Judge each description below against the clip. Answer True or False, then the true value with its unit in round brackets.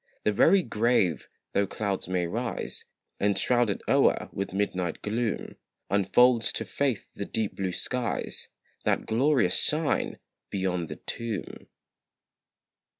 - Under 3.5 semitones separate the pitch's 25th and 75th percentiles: False (4.1 semitones)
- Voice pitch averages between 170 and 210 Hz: False (105 Hz)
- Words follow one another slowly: True (125 wpm)